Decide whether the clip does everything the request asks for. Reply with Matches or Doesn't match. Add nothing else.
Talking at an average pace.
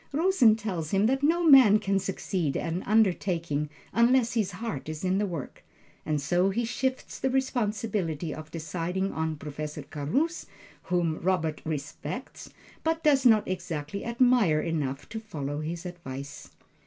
Matches